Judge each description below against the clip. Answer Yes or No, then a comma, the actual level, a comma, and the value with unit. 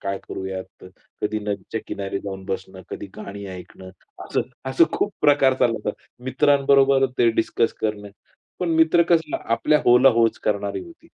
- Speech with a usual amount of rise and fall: No, wide, 6.0 semitones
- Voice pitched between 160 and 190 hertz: No, low, 115 Hz